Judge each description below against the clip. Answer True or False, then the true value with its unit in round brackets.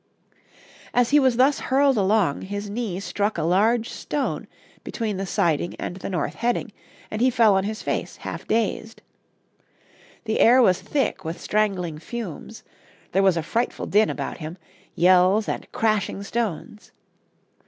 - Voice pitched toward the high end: True (210 Hz)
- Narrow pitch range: False (3.9 semitones)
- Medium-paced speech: True (155 wpm)